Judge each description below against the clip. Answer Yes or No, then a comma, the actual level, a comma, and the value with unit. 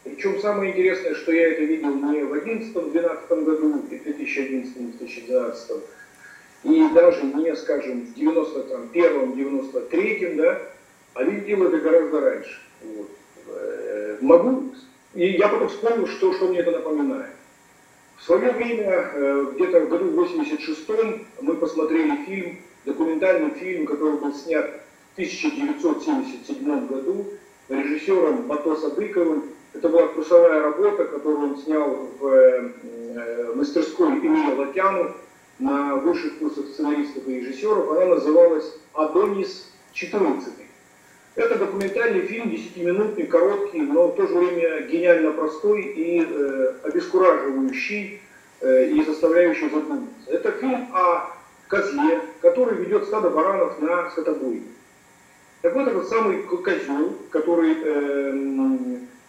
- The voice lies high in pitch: Yes, high, 210 Hz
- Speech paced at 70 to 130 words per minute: Yes, average, 115 wpm